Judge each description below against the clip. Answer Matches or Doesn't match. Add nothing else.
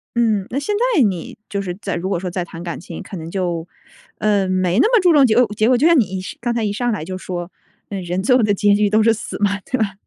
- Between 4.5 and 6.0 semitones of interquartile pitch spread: Doesn't match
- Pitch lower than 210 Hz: Matches